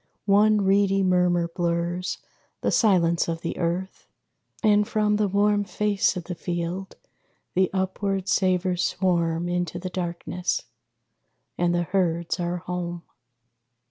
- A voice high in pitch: No, medium, 180 Hz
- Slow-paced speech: Yes, slow, 125 wpm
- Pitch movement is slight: Yes, narrow, 2.2 semitones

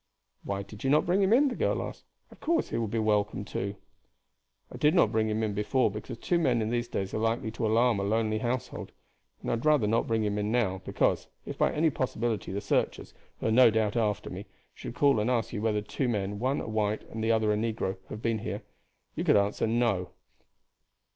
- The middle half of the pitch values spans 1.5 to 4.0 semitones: Yes, narrow, 2.5 semitones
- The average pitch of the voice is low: Yes, low, 110 Hz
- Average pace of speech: No, fast, 235 wpm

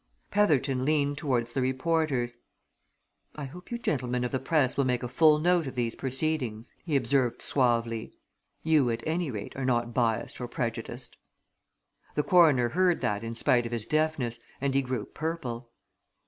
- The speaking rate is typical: Yes, average, 165 wpm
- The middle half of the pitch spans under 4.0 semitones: No, average, 4.3 semitones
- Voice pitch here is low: Yes, low, 130 Hz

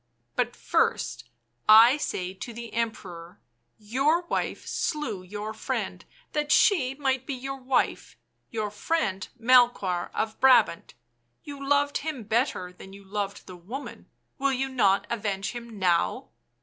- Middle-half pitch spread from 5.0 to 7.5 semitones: Yes, wide, 5.6 semitones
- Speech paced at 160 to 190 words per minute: No, average, 150 wpm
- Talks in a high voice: Yes, high, 230 Hz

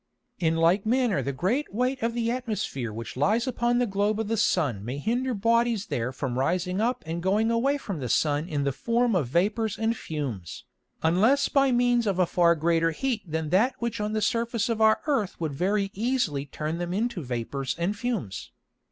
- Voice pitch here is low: No, high, 200 Hz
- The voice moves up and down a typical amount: No, wide, 6.6 semitones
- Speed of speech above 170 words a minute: Yes, average, 200 wpm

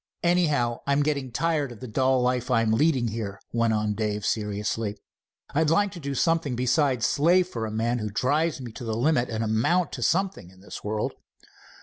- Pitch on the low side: Yes, low, 125 Hz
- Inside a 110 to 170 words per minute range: No, average, 195 wpm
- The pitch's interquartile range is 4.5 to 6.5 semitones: Yes, average, 5.3 semitones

